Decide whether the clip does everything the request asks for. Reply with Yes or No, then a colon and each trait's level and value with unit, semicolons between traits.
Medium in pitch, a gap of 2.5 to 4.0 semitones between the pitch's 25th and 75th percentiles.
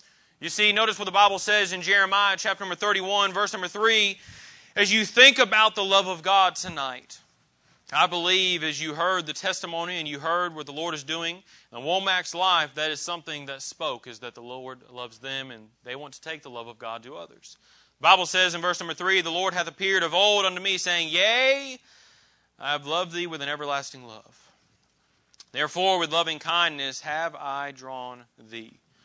No: medium, 175 Hz; average, 4.9 semitones